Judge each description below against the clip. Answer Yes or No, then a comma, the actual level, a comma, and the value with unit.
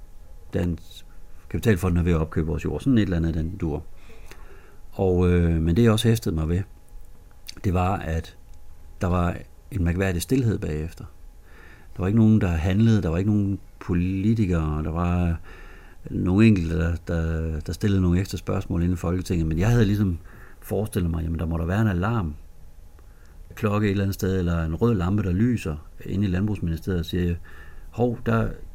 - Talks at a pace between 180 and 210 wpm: Yes, average, 190 wpm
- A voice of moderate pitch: No, very low, 90 Hz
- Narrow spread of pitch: No, average, 3.2 semitones